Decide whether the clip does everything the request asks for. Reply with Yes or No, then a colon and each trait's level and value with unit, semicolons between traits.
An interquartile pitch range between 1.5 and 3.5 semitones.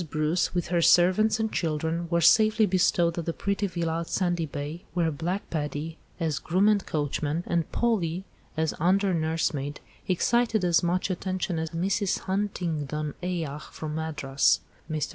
Yes: average, 2.9 semitones